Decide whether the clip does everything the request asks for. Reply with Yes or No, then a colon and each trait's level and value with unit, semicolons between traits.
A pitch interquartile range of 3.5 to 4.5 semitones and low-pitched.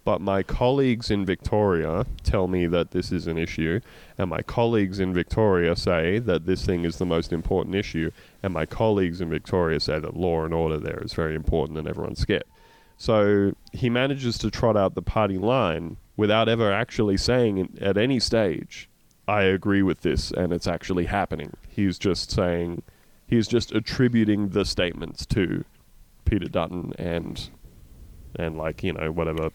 Yes: average, 4.1 semitones; very low, 95 Hz